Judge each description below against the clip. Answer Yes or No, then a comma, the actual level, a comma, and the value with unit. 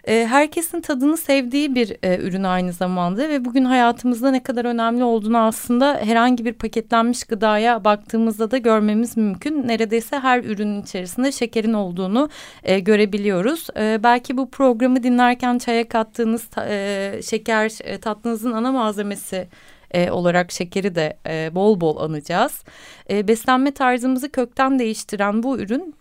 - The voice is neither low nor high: No, high, 230 Hz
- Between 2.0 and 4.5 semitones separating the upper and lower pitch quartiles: Yes, average, 3.4 semitones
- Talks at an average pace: Yes, average, 120 wpm